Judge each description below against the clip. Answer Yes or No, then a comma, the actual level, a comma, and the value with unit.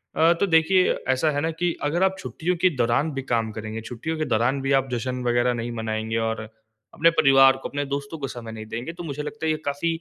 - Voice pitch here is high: No, low, 135 Hz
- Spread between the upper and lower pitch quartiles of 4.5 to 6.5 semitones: Yes, wide, 5.4 semitones